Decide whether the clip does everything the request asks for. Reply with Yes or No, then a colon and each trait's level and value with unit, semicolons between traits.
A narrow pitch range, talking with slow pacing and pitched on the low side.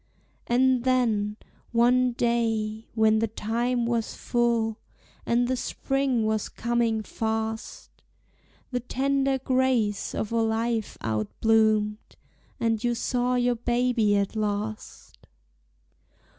No: narrow, 2.1 semitones; slow, 105 wpm; high, 230 Hz